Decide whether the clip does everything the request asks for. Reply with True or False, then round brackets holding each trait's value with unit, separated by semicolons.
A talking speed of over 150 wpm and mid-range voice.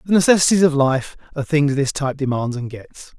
True (205 wpm; 145 Hz)